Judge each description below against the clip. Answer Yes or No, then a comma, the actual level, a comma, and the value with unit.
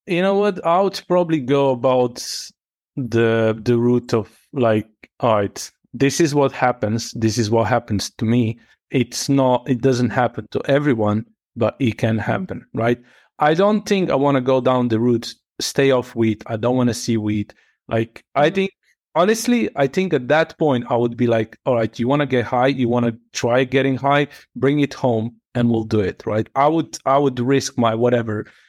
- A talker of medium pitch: No, low, 125 Hz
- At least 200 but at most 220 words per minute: Yes, fast, 205 wpm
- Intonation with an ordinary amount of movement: Yes, average, 3.5 semitones